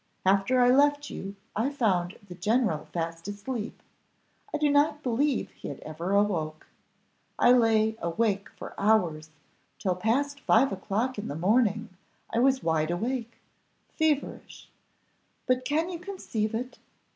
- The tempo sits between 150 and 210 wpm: No, average, 140 wpm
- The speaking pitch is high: Yes, high, 220 Hz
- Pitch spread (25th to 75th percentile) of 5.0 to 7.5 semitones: Yes, wide, 5.6 semitones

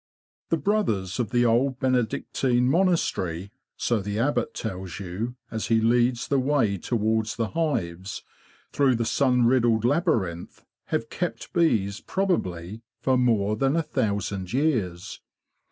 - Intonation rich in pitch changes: No, average, 4.7 semitones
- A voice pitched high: No, low, 115 Hz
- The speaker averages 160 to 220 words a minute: No, slow, 135 wpm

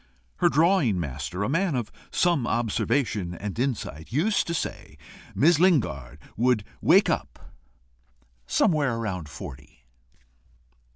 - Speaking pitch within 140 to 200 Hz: No, low, 120 Hz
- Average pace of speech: No, slow, 115 wpm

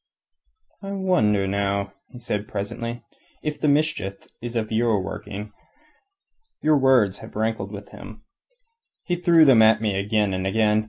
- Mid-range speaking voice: No, low, 110 Hz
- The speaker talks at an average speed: Yes, average, 150 wpm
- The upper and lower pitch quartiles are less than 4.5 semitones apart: Yes, average, 4.1 semitones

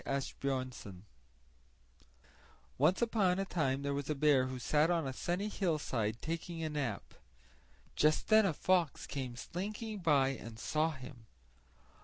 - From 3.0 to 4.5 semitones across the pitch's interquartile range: No, average, 5.0 semitones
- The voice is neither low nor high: Yes, medium, 150 Hz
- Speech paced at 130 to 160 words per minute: Yes, average, 140 wpm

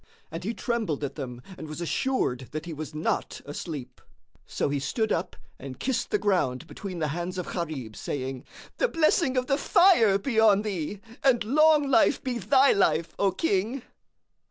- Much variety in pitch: Yes, wide, 8.4 semitones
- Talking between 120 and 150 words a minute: No, average, 180 wpm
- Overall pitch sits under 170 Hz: No, high, 190 Hz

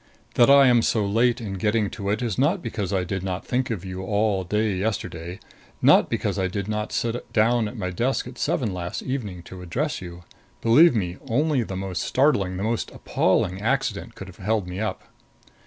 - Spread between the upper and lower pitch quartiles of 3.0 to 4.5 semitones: Yes, average, 4.1 semitones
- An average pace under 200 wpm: No, fast, 205 wpm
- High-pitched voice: No, low, 105 Hz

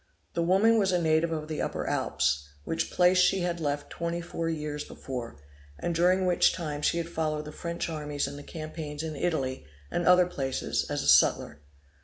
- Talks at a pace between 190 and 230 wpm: Yes, average, 195 wpm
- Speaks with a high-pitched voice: No, medium, 160 Hz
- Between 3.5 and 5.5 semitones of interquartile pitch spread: No, average, 2.8 semitones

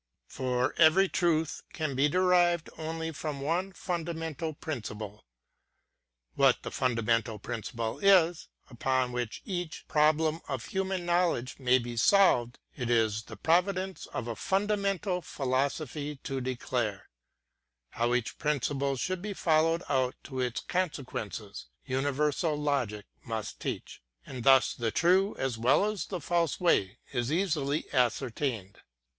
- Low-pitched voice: No, medium, 145 Hz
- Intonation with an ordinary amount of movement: No, wide, 5.9 semitones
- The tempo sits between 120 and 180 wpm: Yes, average, 140 wpm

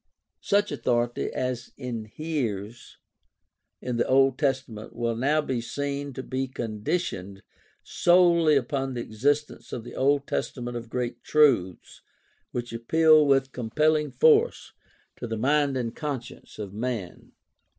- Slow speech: Yes, slow, 130 wpm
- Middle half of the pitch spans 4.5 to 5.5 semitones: No, average, 4.0 semitones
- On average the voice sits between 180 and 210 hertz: No, low, 130 Hz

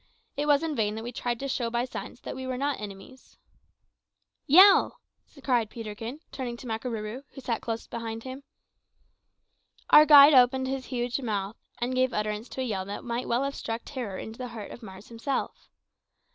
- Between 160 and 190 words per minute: Yes, average, 185 wpm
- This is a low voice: No, high, 240 Hz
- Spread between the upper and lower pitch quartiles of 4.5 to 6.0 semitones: No, average, 2.8 semitones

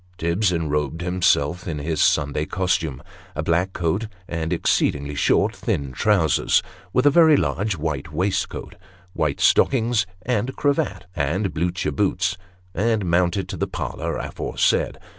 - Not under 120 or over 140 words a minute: Yes, slow, 135 wpm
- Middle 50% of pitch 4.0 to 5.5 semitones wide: Yes, average, 4.9 semitones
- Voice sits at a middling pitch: No, very low, 85 Hz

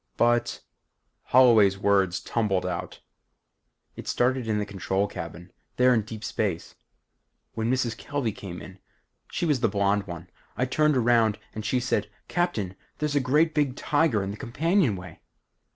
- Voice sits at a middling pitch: No, low, 115 Hz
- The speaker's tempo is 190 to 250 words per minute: No, average, 155 wpm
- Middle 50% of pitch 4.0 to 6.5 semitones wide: Yes, average, 4.6 semitones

